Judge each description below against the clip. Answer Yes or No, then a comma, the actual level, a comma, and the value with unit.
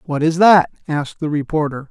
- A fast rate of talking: No, average, 190 wpm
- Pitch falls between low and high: Yes, medium, 155 Hz